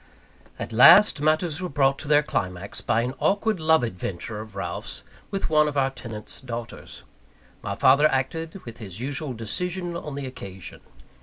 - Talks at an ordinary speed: Yes, average, 165 wpm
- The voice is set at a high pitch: No, low, 135 Hz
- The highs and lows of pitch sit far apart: Yes, wide, 5.9 semitones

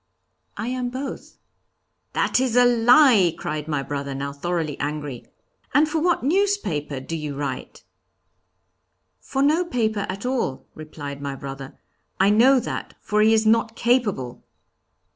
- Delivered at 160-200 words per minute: No, average, 145 wpm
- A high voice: Yes, high, 205 Hz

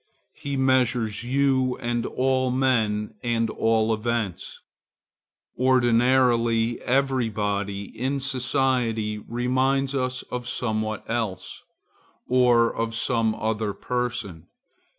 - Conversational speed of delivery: No, slow, 95 wpm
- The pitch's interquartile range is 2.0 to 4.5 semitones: Yes, narrow, 2.6 semitones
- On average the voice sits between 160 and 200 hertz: No, low, 120 Hz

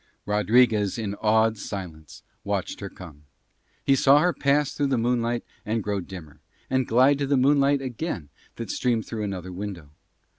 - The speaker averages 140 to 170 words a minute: Yes, average, 160 wpm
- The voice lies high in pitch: No, low, 115 Hz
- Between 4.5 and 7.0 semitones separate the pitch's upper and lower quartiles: Yes, average, 5.2 semitones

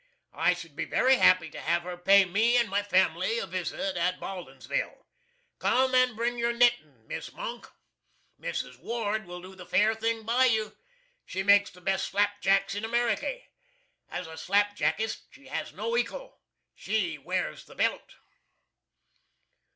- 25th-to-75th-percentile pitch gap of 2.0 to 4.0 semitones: No, average, 4.6 semitones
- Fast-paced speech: No, average, 160 wpm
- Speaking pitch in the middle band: No, high, 205 Hz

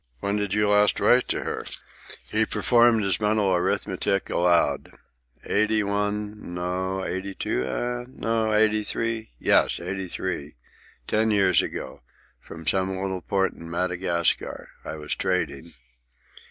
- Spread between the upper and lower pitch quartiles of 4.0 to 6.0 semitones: No, average, 3.0 semitones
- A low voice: Yes, very low, 95 Hz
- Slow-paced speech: Yes, slow, 125 wpm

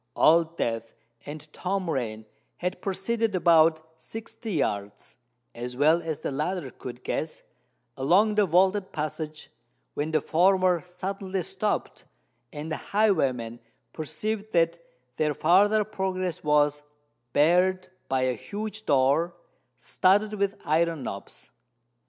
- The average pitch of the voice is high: No, medium, 165 Hz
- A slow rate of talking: Yes, slow, 120 wpm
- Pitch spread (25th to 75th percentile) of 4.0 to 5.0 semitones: Yes, average, 4.5 semitones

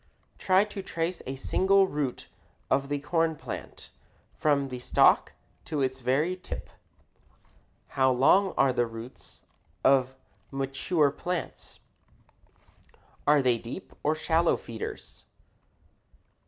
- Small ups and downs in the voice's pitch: No, average, 4.3 semitones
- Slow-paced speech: Yes, slow, 115 wpm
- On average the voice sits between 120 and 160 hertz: Yes, medium, 140 Hz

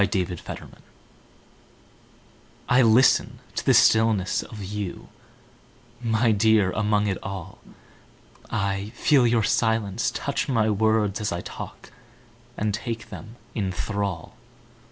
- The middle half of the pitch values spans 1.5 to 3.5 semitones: Yes, narrow, 2.4 semitones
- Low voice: Yes, low, 105 Hz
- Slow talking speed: Yes, slow, 100 wpm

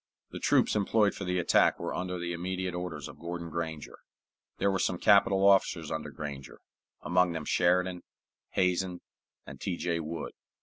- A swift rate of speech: No, average, 165 wpm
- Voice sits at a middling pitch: No, very low, 90 Hz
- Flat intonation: Yes, narrow, 1.9 semitones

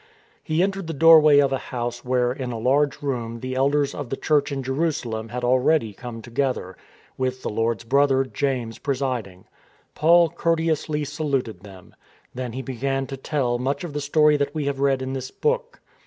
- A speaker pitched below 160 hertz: Yes, low, 135 Hz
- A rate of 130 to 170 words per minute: No, average, 185 wpm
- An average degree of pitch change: Yes, average, 3.1 semitones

